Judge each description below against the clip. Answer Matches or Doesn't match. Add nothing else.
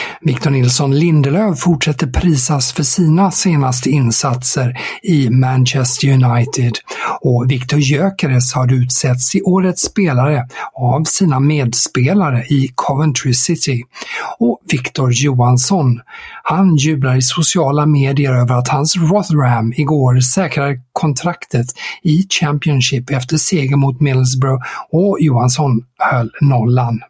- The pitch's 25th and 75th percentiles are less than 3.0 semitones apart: Doesn't match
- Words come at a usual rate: Doesn't match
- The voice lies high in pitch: Doesn't match